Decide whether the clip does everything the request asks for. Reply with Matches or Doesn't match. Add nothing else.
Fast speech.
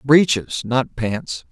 Doesn't match